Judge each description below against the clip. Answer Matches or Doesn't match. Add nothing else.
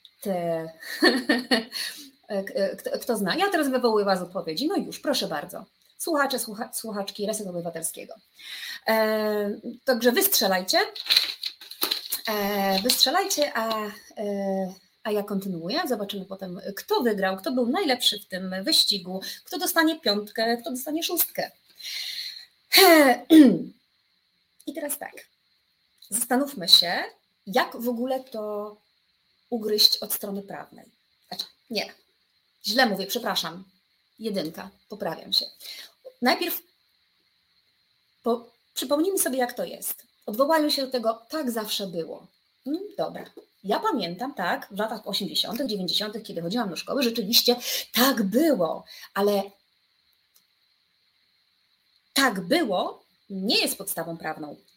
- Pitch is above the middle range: Matches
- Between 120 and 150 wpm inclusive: Doesn't match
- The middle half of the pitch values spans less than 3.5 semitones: Doesn't match